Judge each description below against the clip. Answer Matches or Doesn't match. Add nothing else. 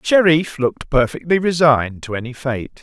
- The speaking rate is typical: Matches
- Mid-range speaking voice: Matches